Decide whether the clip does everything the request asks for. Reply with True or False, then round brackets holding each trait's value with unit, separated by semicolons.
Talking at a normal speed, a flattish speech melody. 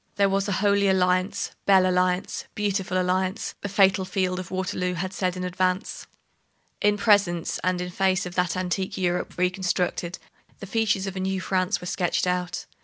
True (175 wpm; 1.2 semitones)